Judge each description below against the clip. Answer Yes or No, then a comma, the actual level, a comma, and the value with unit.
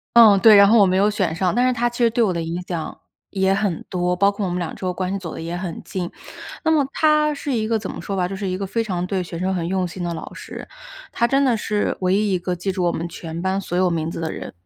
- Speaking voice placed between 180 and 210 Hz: Yes, high, 190 Hz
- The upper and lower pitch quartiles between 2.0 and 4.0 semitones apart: Yes, average, 3.3 semitones